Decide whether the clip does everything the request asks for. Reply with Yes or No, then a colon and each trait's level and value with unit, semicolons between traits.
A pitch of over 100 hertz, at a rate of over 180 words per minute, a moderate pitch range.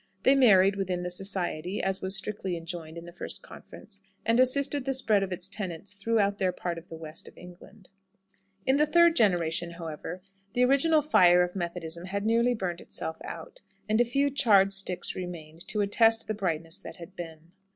Yes: high, 190 Hz; average, 190 wpm; average, 4.4 semitones